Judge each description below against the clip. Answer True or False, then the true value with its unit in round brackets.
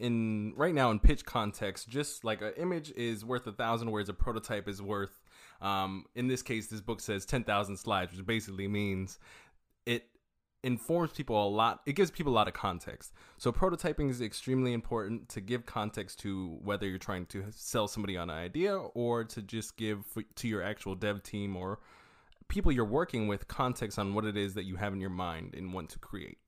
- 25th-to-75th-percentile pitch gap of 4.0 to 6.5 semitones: False (3.1 semitones)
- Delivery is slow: False (205 wpm)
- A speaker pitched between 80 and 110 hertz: True (105 Hz)